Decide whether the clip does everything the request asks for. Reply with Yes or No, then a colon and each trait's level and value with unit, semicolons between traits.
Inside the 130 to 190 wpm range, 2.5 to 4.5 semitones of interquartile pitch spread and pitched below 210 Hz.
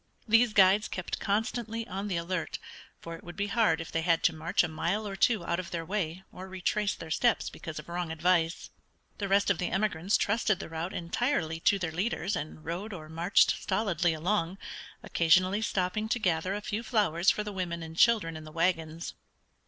No: average, 200 wpm; average, 3.9 semitones; medium, 185 Hz